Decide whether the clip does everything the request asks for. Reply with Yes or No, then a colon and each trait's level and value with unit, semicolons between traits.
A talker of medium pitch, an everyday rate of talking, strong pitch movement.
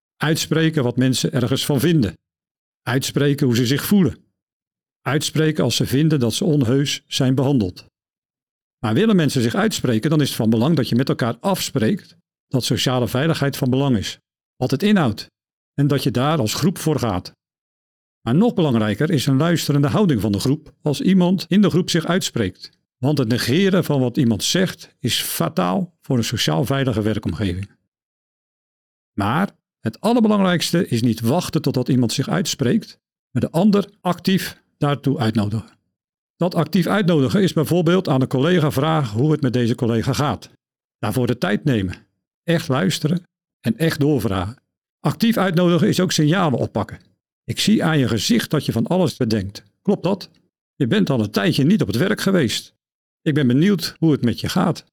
Yes: medium, 145 Hz; average, 175 wpm; wide, 5.8 semitones